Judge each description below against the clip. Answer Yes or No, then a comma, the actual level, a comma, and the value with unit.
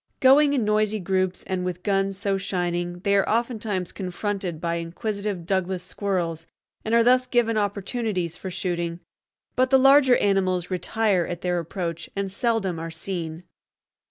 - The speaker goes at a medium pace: Yes, average, 155 wpm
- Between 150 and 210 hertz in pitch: Yes, high, 190 Hz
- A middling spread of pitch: Yes, average, 3.5 semitones